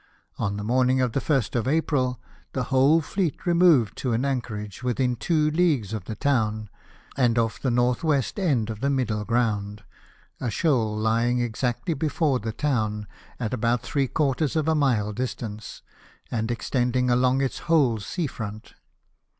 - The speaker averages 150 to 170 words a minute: Yes, average, 165 wpm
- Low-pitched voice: Yes, low, 125 Hz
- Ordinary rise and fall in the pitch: Yes, average, 3.9 semitones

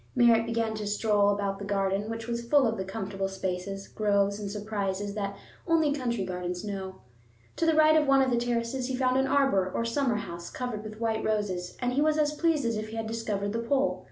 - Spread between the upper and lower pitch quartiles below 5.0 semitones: Yes, average, 3.9 semitones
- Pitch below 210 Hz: No, high, 220 Hz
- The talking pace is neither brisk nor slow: No, fast, 225 wpm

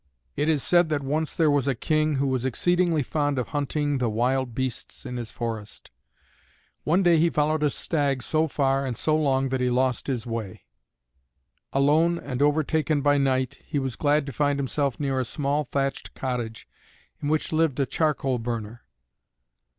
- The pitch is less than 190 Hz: Yes, medium, 140 Hz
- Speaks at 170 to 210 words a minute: Yes, average, 180 wpm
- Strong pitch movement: No, average, 2.9 semitones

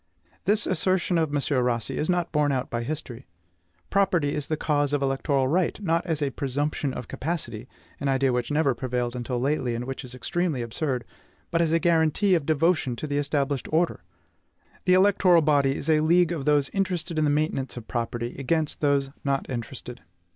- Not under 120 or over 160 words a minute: No, average, 190 wpm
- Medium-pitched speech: Yes, medium, 145 Hz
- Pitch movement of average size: Yes, average, 4.0 semitones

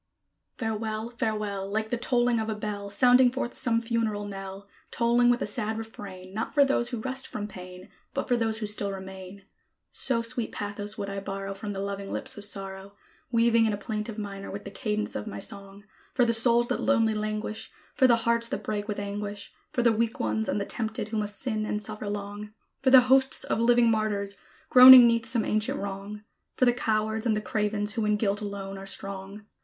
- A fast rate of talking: Yes, fast, 210 wpm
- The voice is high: Yes, high, 215 Hz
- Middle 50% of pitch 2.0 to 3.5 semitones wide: Yes, narrow, 2.5 semitones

